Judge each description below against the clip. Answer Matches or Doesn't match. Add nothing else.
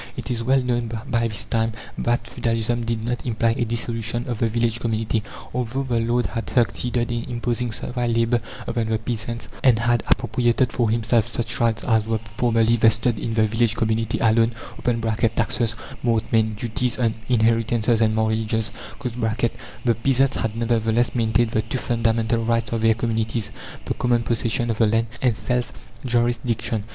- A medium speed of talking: Matches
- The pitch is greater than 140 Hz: Doesn't match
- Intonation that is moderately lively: Doesn't match